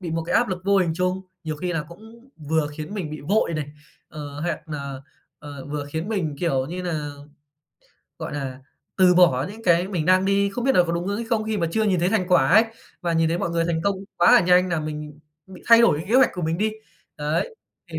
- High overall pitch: No, medium, 170 Hz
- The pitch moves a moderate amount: Yes, average, 4.3 semitones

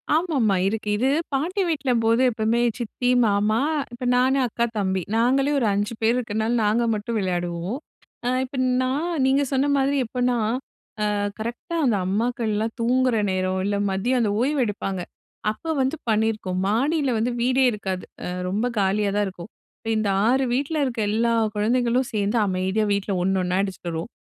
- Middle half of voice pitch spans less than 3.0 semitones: No, average, 3.9 semitones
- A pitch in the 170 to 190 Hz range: No, high, 225 Hz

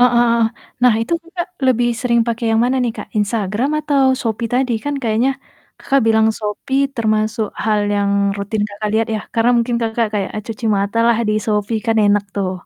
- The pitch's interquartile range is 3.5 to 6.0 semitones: No, narrow, 2.6 semitones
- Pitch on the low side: No, high, 225 Hz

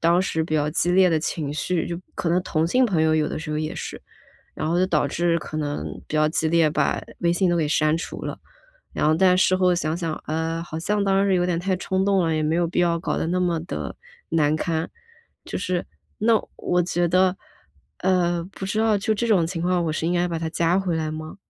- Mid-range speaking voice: Yes, medium, 170 Hz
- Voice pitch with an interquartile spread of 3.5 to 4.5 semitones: No, narrow, 2.5 semitones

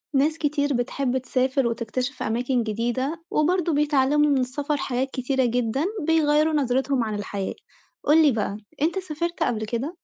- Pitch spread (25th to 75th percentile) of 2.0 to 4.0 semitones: Yes, average, 3.6 semitones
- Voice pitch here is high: Yes, very high, 270 Hz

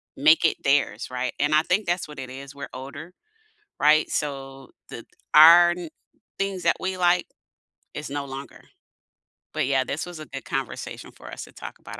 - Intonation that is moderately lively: Yes, average, 4.2 semitones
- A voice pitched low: No, medium, 145 Hz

